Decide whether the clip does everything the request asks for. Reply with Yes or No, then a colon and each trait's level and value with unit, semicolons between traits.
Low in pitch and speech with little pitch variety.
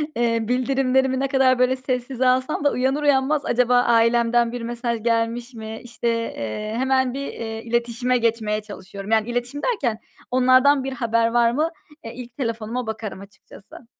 No: high, 240 Hz; narrow, 2.1 semitones